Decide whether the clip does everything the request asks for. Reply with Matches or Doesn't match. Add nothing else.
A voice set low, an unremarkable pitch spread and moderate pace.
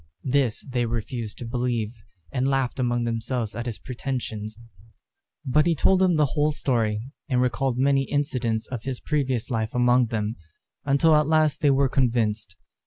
Matches